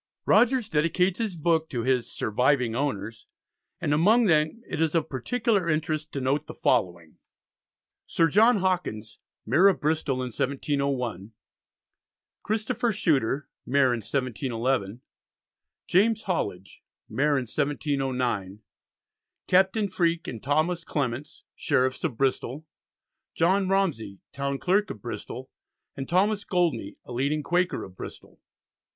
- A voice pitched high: No, medium, 145 Hz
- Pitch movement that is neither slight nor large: No, wide, 6.2 semitones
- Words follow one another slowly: Yes, slow, 125 wpm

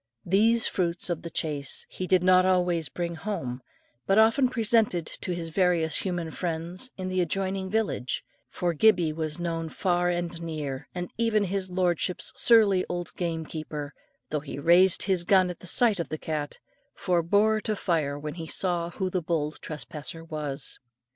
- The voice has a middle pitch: Yes, medium, 175 Hz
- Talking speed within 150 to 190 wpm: Yes, average, 165 wpm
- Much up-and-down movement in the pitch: No, average, 2.9 semitones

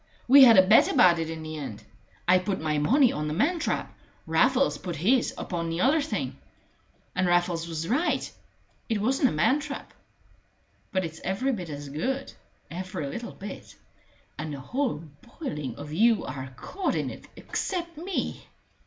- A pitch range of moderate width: No, wide, 8.8 semitones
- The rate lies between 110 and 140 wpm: No, average, 170 wpm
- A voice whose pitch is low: No, medium, 185 Hz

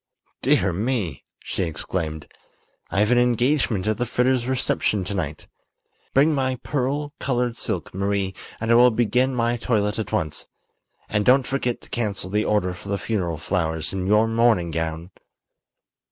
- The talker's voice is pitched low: Yes, low, 110 Hz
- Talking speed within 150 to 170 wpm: Yes, average, 155 wpm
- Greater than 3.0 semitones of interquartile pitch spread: Yes, average, 5.1 semitones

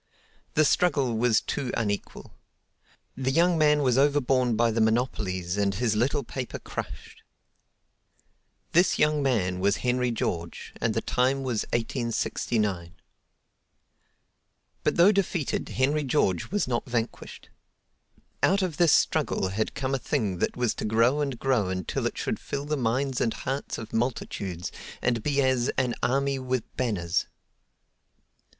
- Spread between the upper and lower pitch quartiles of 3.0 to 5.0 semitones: Yes, average, 4.0 semitones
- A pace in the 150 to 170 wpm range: No, average, 140 wpm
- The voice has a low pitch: Yes, low, 125 Hz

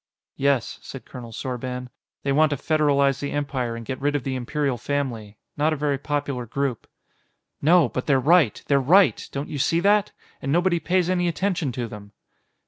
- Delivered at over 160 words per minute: Yes, average, 185 wpm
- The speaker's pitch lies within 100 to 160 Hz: Yes, medium, 140 Hz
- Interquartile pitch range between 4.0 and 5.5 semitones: No, average, 3.5 semitones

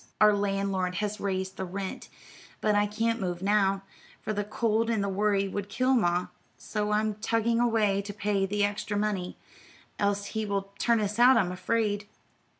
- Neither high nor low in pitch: No, high, 205 Hz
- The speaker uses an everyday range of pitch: No, narrow, 1.6 semitones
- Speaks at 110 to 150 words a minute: No, average, 175 wpm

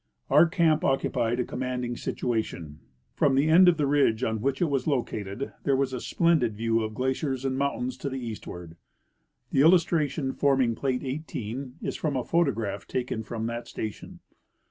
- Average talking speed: Yes, average, 170 wpm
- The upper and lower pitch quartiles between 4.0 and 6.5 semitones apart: No, average, 3.5 semitones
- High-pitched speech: No, low, 130 Hz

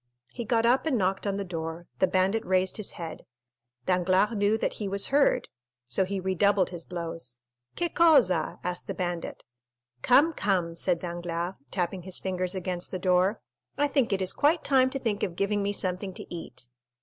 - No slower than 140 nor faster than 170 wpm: No, average, 185 wpm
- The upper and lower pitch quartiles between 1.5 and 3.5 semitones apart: Yes, average, 3.1 semitones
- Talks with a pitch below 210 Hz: Yes, high, 190 Hz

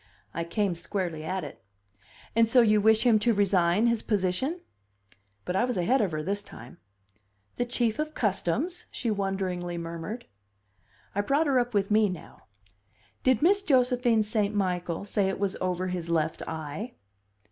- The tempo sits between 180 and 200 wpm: No, average, 165 wpm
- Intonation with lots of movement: No, average, 4.9 semitones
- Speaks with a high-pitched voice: Yes, high, 205 Hz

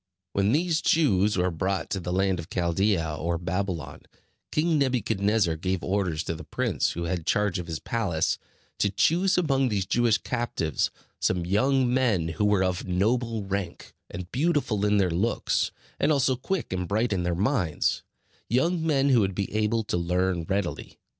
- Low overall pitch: Yes, low, 100 Hz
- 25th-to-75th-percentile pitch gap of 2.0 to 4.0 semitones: No, wide, 5.5 semitones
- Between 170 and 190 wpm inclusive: Yes, average, 175 wpm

